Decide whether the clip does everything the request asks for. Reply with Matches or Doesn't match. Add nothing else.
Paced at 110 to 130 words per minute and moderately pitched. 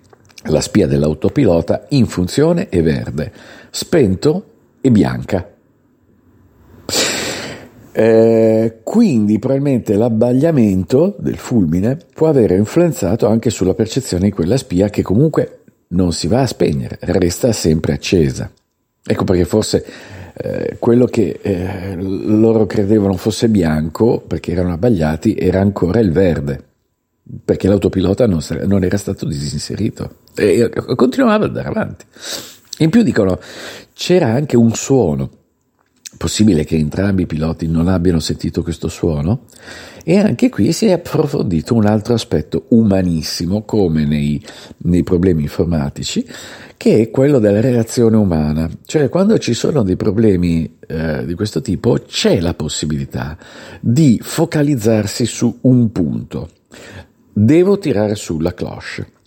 Doesn't match